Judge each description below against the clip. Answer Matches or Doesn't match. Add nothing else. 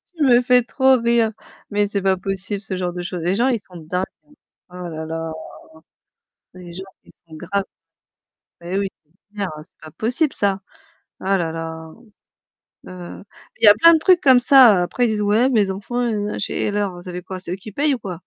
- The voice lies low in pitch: Doesn't match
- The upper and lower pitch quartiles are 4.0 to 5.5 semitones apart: Matches